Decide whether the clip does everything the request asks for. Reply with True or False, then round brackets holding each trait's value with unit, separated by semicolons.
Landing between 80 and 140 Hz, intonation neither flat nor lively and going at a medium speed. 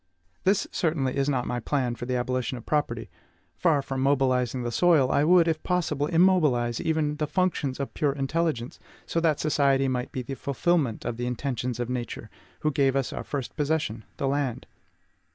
True (135 Hz; 3.6 semitones; 185 wpm)